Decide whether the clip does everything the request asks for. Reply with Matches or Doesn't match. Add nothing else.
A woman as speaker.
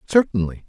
Doesn't match